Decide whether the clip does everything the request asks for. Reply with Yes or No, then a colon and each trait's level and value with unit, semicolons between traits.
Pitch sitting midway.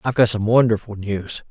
No: low, 110 Hz